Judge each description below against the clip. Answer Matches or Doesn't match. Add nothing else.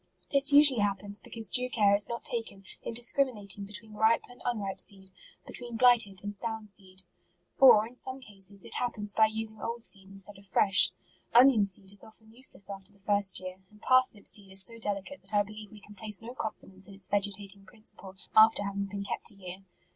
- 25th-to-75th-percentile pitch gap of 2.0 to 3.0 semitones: Matches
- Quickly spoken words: Matches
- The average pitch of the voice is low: Doesn't match